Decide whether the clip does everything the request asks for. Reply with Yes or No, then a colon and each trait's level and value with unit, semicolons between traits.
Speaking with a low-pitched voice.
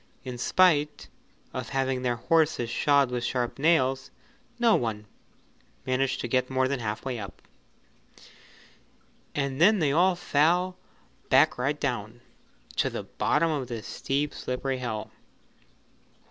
Yes: low, 130 Hz